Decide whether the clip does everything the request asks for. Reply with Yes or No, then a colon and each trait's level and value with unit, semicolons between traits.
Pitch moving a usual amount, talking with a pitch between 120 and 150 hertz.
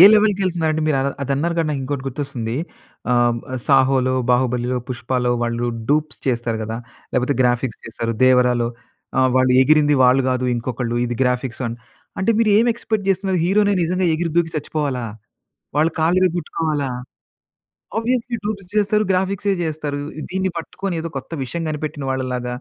No: wide, 6.0 semitones; medium, 145 Hz